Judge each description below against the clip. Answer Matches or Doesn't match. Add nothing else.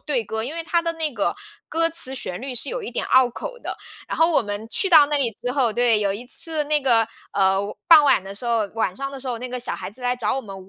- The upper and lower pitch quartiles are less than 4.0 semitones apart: Doesn't match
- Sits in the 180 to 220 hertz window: Doesn't match